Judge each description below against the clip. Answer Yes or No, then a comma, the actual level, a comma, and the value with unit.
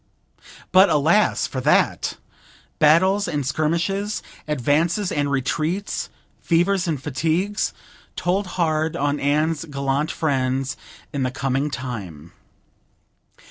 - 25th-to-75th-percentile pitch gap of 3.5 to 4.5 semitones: Yes, average, 4.1 semitones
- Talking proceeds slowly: Yes, slow, 100 wpm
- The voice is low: No, medium, 155 Hz